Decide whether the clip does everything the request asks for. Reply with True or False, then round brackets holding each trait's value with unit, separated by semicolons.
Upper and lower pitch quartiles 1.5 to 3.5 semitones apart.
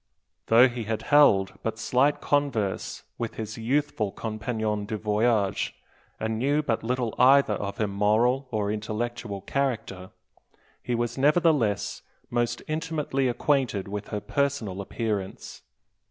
False (4.0 semitones)